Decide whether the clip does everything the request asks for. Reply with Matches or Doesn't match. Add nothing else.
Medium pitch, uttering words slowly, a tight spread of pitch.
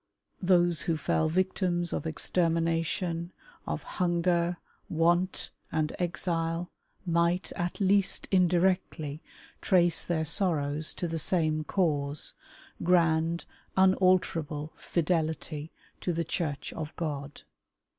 Matches